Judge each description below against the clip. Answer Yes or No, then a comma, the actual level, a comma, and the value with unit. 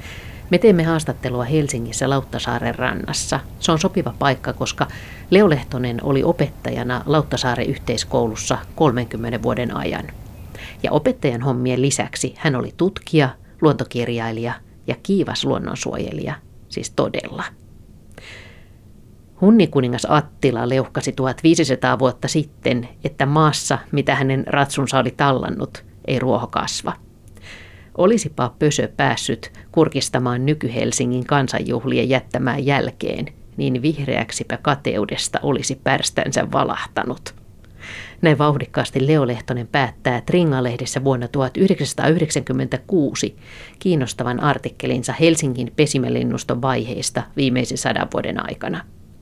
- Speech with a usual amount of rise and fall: Yes, average, 3.8 semitones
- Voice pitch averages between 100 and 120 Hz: No, low, 130 Hz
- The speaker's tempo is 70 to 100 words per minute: Yes, slow, 95 wpm